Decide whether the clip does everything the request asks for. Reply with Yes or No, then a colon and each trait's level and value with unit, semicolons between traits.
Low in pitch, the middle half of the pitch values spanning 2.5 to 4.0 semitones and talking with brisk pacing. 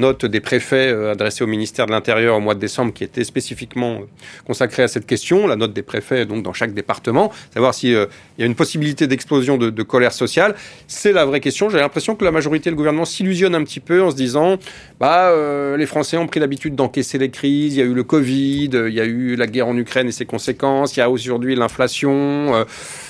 Yes: low, 130 Hz; average, 3.6 semitones; fast, 235 wpm